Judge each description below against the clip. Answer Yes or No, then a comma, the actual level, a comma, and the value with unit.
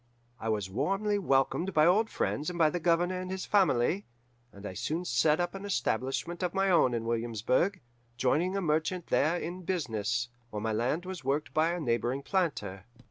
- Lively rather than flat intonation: Yes, wide, 7.2 semitones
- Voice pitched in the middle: Yes, medium, 160 Hz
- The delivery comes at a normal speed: Yes, average, 190 wpm